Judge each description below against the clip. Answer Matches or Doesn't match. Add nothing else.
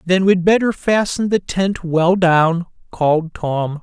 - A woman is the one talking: Doesn't match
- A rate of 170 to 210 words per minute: Doesn't match